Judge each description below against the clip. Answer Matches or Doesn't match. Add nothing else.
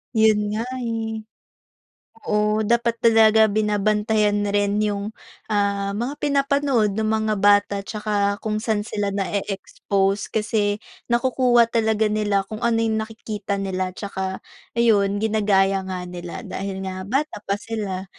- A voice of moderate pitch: Doesn't match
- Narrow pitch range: Matches